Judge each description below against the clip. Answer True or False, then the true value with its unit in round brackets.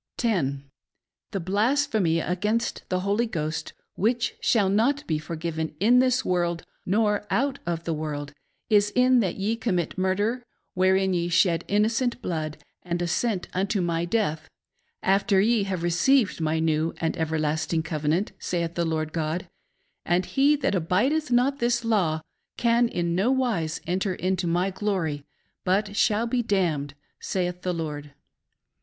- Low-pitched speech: False (185 Hz)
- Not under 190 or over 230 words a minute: False (155 wpm)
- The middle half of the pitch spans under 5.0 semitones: False (5.3 semitones)